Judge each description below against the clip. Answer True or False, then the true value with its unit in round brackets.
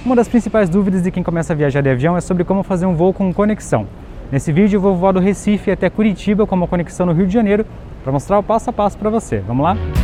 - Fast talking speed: True (270 wpm)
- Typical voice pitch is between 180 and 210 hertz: True (190 Hz)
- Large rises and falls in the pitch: False (3.0 semitones)